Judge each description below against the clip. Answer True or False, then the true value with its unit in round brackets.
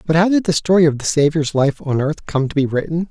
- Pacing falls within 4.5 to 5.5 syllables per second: False (6.0 syllables/s)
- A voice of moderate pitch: True (155 Hz)